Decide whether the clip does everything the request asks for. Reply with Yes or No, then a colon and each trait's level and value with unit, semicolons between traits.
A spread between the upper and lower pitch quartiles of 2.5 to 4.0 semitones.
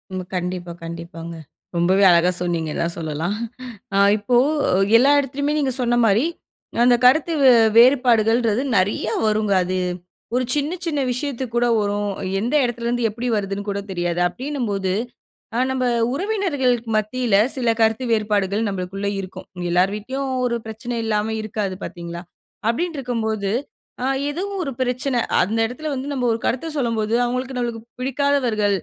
No: average, 4.5 semitones